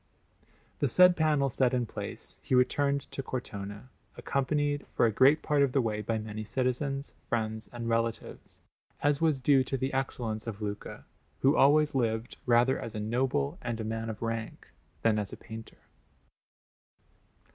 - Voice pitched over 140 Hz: No, low, 125 Hz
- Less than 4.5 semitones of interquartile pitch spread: Yes, average, 3.8 semitones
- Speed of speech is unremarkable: Yes, average, 165 wpm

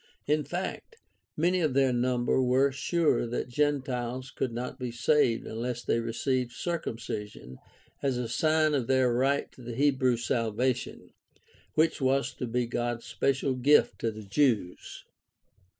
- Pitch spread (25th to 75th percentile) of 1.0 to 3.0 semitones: Yes, average, 2.7 semitones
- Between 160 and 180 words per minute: No, average, 145 wpm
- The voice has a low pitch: Yes, low, 125 Hz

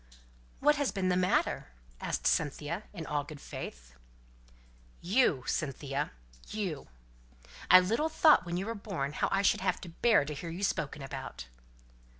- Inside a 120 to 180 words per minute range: Yes, average, 155 wpm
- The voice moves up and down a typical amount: No, wide, 5.7 semitones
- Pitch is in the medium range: Yes, medium, 175 Hz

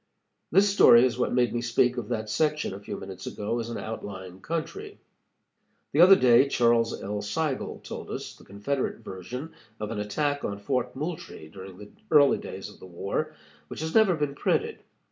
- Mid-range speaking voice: No, low, 120 Hz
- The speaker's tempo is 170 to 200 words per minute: Yes, average, 185 wpm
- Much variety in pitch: Yes, wide, 6.4 semitones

